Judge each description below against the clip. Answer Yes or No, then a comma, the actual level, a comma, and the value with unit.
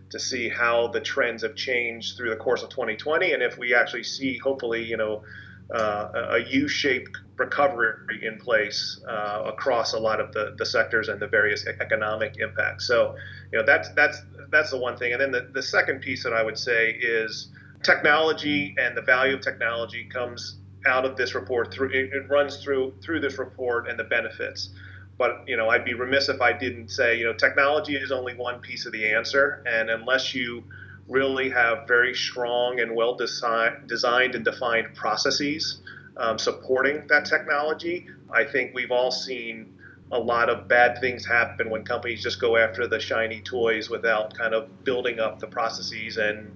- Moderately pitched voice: No, low, 125 Hz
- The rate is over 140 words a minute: Yes, average, 190 wpm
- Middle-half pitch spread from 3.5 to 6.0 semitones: Yes, average, 4.2 semitones